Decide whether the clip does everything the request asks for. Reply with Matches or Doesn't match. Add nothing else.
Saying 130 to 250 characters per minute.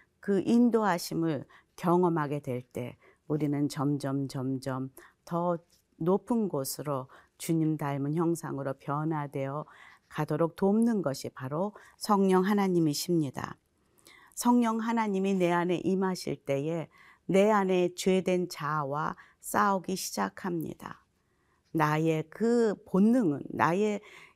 Matches